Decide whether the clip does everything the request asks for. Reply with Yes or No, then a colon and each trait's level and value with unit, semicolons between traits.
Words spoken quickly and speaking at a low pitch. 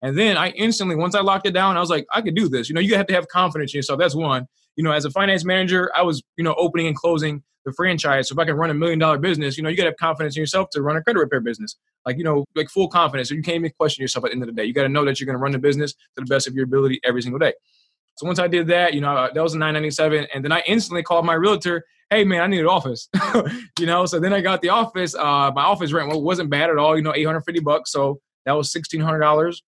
No: fast, 310 wpm; medium, 160 Hz